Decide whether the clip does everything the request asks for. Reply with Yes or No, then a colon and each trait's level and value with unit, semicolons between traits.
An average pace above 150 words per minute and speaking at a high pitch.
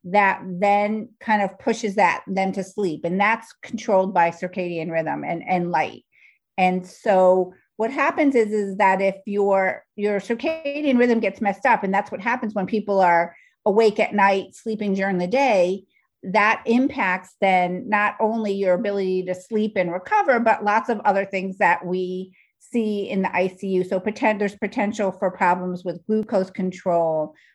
Yes: average, 170 wpm; high, 195 Hz